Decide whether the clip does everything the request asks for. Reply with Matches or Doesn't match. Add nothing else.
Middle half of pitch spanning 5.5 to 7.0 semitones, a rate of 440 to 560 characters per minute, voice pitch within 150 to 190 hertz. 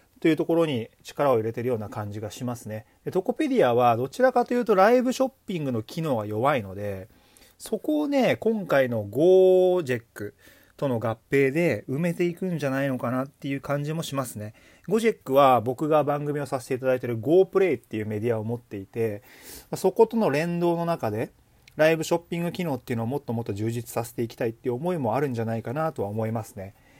Doesn't match